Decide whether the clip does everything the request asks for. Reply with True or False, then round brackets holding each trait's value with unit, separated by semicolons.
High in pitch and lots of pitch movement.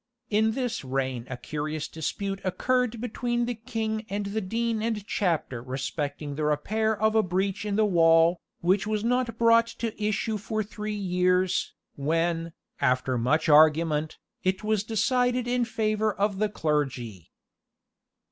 True (200 Hz; 5.9 semitones)